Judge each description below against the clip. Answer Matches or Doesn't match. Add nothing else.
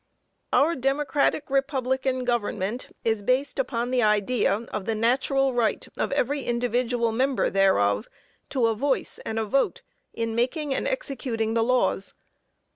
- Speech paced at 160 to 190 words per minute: Doesn't match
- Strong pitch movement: Doesn't match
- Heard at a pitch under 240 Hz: Doesn't match